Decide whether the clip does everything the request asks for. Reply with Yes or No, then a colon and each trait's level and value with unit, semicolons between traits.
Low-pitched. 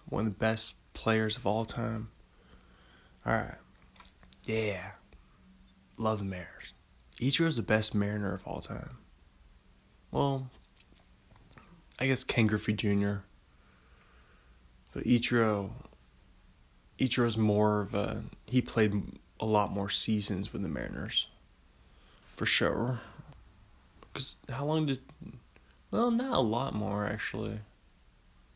Yes: low, 105 Hz